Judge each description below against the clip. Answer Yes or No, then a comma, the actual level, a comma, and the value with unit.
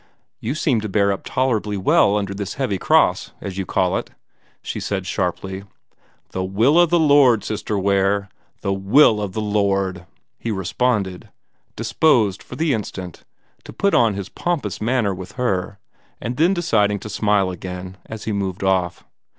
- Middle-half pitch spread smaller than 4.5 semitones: Yes, average, 3.6 semitones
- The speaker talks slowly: No, average, 165 wpm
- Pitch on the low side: Yes, low, 100 Hz